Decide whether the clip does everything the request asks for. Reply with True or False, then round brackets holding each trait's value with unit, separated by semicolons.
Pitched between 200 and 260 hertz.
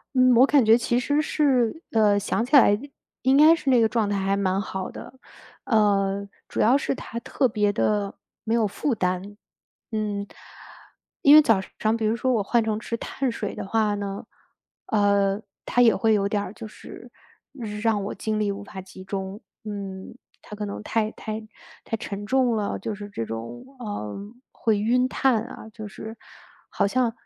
True (215 Hz)